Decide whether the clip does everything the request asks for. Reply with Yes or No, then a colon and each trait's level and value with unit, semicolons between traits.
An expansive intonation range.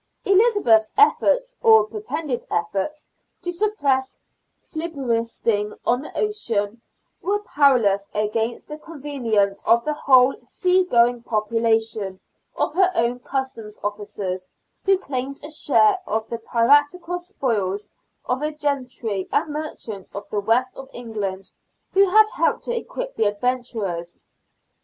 Yes: wide, 7.0 semitones